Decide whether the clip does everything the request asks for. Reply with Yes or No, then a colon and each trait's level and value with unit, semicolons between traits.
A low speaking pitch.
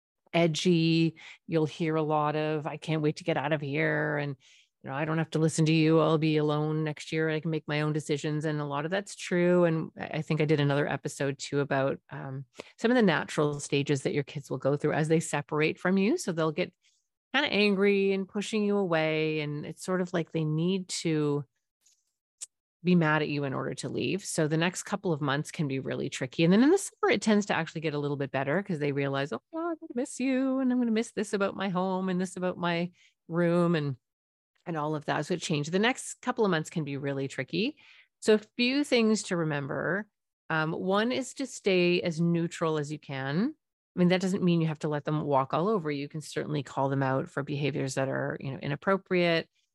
No: medium, 160 Hz